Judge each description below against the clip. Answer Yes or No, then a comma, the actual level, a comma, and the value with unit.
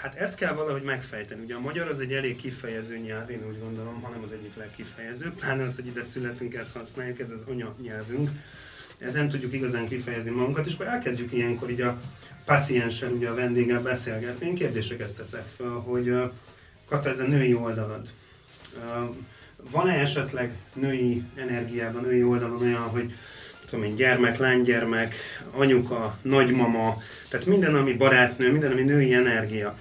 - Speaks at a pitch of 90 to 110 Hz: No, low, 125 Hz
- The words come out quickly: Yes, fast, 160 wpm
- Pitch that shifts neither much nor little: No, narrow, 2.3 semitones